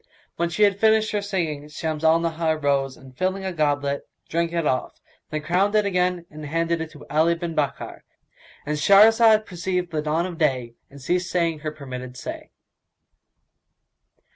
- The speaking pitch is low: No, medium, 165 Hz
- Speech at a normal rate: Yes, average, 165 wpm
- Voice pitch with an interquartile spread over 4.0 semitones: No, average, 3.4 semitones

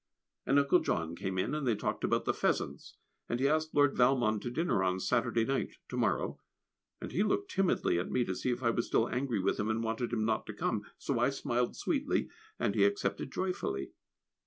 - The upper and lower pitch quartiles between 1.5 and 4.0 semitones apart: No, average, 4.9 semitones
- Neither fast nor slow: No, fast, 215 wpm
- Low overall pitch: Yes, low, 120 Hz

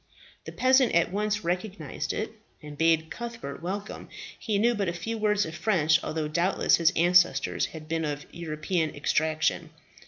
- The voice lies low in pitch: No, medium, 170 Hz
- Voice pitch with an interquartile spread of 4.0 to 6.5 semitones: Yes, average, 4.8 semitones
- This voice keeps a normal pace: Yes, average, 160 wpm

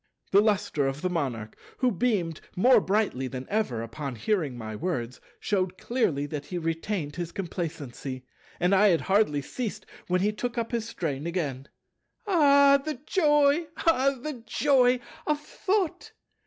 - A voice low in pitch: No, medium, 185 Hz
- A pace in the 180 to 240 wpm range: No, average, 155 wpm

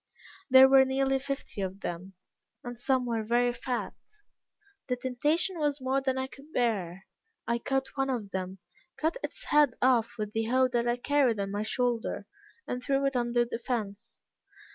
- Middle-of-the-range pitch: No, high, 245 Hz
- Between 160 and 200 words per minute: Yes, average, 175 wpm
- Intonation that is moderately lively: Yes, average, 3.1 semitones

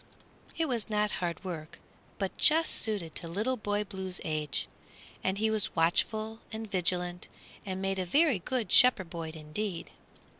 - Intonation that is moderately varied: Yes, average, 4.1 semitones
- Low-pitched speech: No, high, 195 Hz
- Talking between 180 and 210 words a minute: No, average, 155 wpm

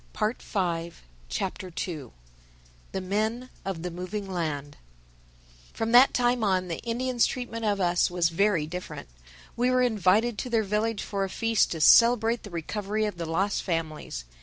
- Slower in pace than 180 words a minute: Yes, average, 160 wpm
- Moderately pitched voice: No, high, 200 Hz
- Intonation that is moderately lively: Yes, average, 4.6 semitones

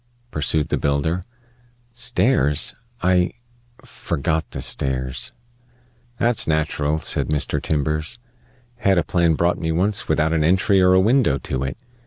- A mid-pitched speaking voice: No, very low, 80 Hz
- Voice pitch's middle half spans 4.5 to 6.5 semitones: No, average, 3.7 semitones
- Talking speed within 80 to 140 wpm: Yes, slow, 135 wpm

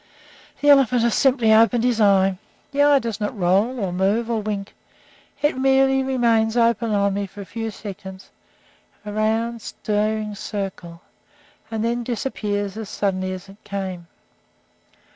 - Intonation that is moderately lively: Yes, average, 3.0 semitones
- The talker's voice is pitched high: Yes, high, 215 Hz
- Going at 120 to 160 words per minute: Yes, average, 150 wpm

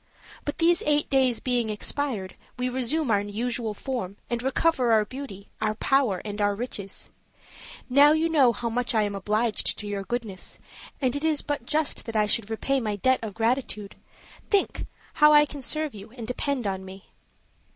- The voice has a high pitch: Yes, high, 240 Hz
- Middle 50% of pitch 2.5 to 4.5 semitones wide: No, average, 4.9 semitones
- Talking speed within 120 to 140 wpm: No, average, 185 wpm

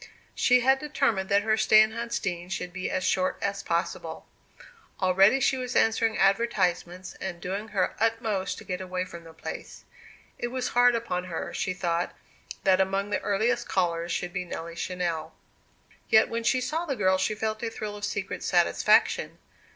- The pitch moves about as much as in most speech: Yes, average, 3.8 semitones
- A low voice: No, high, 195 Hz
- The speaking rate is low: No, average, 175 wpm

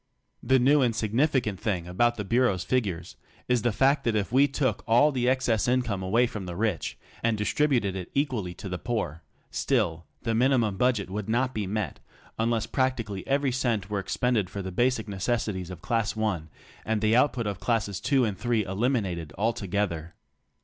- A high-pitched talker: No, low, 110 Hz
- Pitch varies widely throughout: No, average, 4.3 semitones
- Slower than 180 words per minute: No, average, 185 wpm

